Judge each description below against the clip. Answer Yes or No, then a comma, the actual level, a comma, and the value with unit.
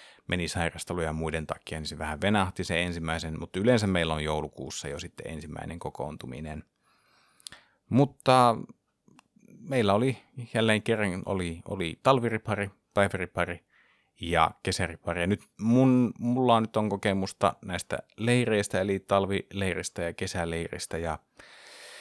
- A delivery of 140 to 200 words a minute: No, average, 120 wpm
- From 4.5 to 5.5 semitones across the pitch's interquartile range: Yes, average, 5.0 semitones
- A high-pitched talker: No, very low, 95 Hz